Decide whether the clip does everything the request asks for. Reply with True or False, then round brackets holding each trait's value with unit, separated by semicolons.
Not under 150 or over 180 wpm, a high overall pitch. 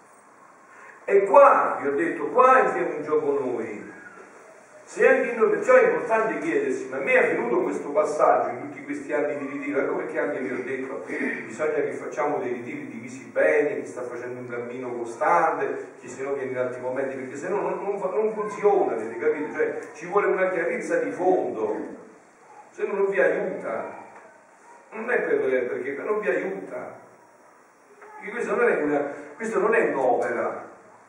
True (170 wpm; 220 Hz)